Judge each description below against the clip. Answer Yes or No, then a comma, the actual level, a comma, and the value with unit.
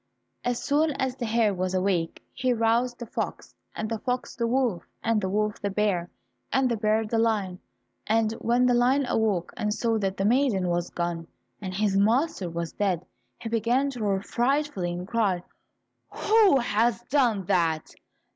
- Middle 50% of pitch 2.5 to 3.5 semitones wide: No, average, 4.3 semitones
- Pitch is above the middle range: Yes, high, 220 Hz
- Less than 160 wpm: No, average, 175 wpm